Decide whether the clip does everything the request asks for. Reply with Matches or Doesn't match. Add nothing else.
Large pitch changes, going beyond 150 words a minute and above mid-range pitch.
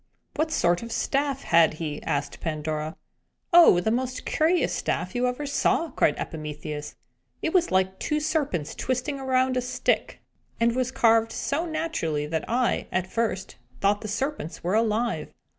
Matches